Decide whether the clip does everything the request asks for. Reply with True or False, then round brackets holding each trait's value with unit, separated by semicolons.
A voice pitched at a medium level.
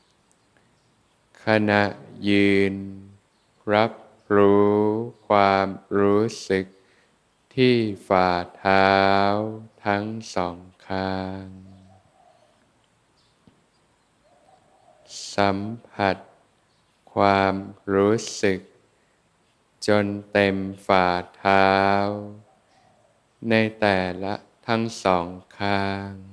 False (100 Hz)